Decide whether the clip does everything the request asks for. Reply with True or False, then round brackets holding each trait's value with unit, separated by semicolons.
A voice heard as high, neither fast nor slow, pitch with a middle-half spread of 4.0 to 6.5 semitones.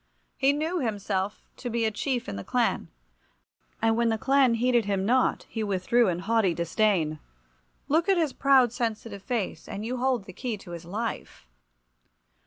True (225 Hz; 175 wpm; 4.3 semitones)